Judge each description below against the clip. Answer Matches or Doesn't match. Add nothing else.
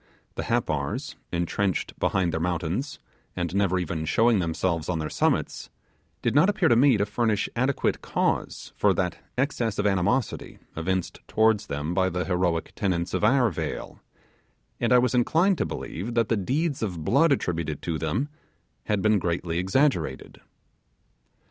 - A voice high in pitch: Doesn't match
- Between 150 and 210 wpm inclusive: Matches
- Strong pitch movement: Matches